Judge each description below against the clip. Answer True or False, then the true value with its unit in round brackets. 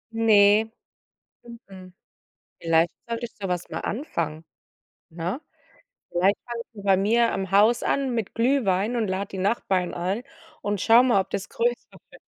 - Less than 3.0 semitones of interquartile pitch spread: False (3.9 semitones)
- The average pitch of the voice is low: False (205 Hz)